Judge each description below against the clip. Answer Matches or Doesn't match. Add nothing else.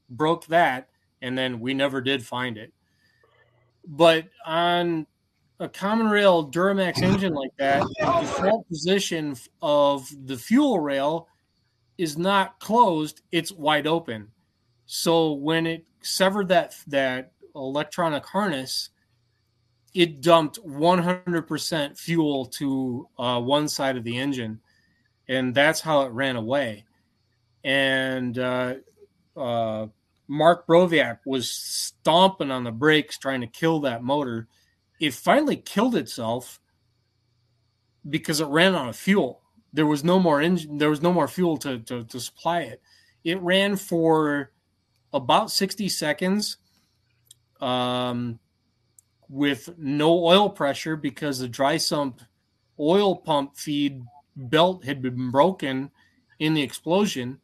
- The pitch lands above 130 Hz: Matches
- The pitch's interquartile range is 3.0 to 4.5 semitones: Doesn't match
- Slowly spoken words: Matches